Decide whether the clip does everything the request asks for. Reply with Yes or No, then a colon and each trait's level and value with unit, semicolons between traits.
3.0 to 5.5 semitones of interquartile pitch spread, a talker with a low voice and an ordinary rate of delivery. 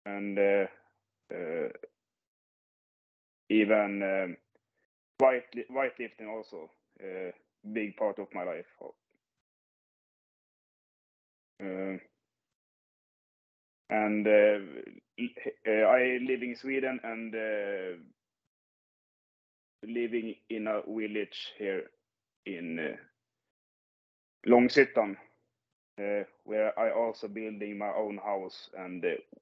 No: average, 3.5 semitones; low, 110 Hz; slow, 85 wpm